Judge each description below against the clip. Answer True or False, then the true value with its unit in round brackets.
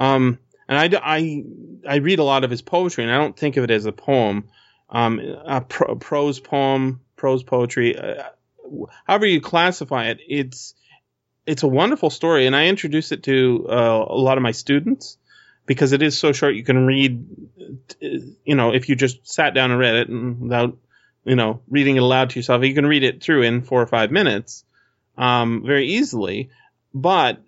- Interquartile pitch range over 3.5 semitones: False (2.8 semitones)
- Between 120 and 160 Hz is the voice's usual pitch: True (130 Hz)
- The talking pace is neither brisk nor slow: True (195 wpm)